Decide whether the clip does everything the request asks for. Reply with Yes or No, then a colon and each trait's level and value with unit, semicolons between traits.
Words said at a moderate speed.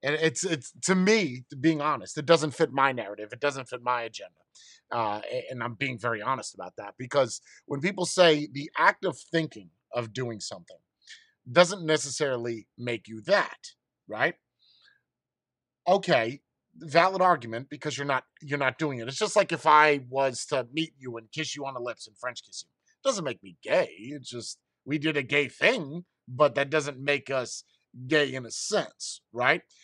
Yes: average, 185 wpm